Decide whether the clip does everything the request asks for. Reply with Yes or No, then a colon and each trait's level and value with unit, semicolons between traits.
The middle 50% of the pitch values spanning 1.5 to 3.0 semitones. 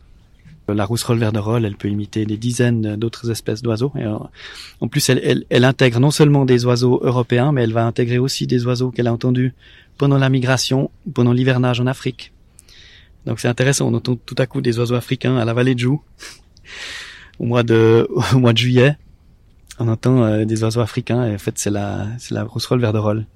Yes: narrow, 2.4 semitones